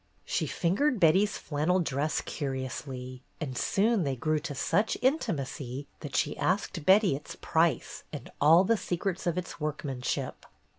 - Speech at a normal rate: Yes, average, 145 wpm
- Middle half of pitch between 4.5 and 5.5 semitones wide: Yes, average, 5.2 semitones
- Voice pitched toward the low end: No, medium, 160 Hz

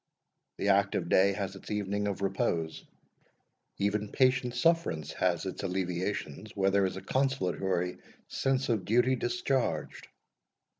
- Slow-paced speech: Yes, slow, 130 wpm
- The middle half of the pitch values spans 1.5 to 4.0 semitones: No, average, 4.4 semitones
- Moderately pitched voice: No, low, 100 Hz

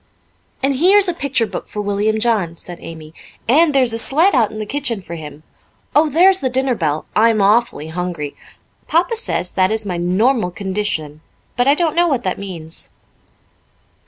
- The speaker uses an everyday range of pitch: No, wide, 7.5 semitones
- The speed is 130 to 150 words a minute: No, average, 185 wpm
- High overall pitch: Yes, high, 220 Hz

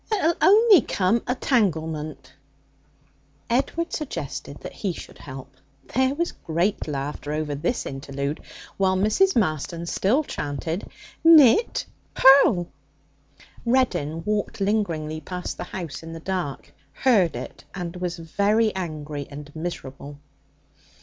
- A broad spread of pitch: Yes, wide, 7.1 semitones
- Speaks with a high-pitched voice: No, medium, 180 Hz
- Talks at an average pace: No, slow, 120 wpm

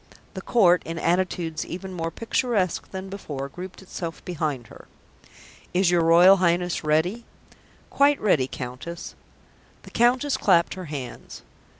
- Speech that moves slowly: Yes, slow, 130 wpm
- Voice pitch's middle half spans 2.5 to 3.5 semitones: Yes, average, 2.8 semitones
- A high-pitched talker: No, medium, 175 Hz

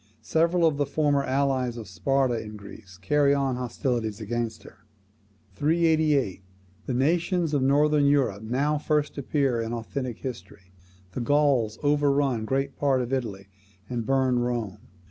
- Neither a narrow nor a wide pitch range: Yes, average, 3.8 semitones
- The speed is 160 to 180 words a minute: No, average, 145 wpm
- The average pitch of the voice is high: No, low, 130 Hz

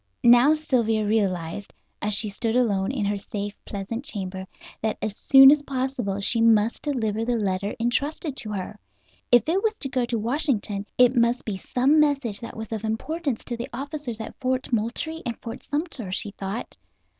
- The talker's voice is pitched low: No, high, 230 Hz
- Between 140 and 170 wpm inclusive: No, average, 180 wpm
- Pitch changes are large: No, average, 4.3 semitones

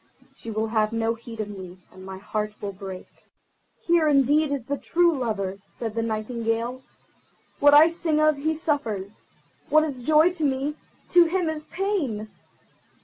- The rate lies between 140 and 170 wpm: Yes, average, 160 wpm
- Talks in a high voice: Yes, very high, 255 Hz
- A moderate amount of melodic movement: No, wide, 6.2 semitones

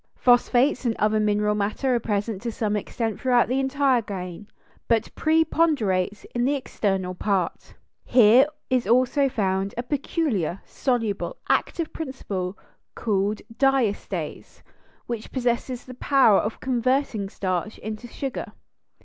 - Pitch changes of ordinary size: Yes, average, 4.1 semitones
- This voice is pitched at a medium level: No, high, 230 Hz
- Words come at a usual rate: No, slow, 130 wpm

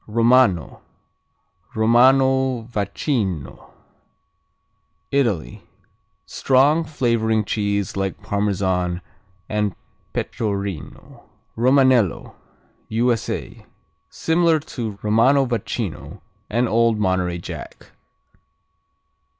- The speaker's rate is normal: No, slow, 65 wpm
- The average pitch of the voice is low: Yes, low, 110 Hz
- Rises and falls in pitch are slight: No, average, 4.4 semitones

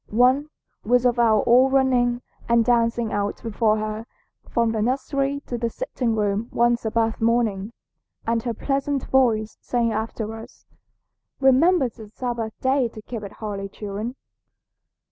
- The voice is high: Yes, high, 235 Hz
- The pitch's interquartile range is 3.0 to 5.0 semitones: No, narrow, 2.5 semitones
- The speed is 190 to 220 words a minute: No, average, 145 wpm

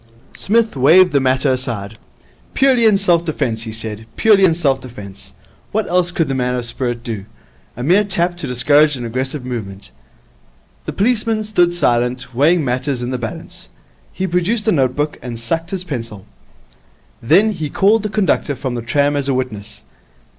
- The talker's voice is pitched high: No, medium, 140 Hz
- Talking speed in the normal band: Yes, average, 175 wpm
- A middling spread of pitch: No, wide, 6.6 semitones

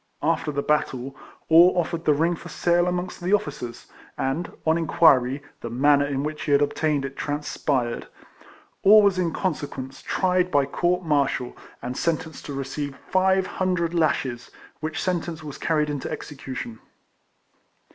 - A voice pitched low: No, medium, 150 Hz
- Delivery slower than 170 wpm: Yes, average, 150 wpm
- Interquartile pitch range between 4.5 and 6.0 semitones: No, average, 4.0 semitones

